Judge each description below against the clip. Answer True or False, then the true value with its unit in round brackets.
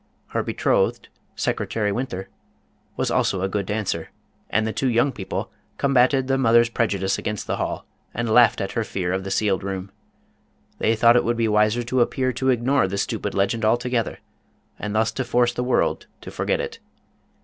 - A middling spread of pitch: True (3.5 semitones)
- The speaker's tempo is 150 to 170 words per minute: False (190 wpm)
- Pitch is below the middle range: True (115 Hz)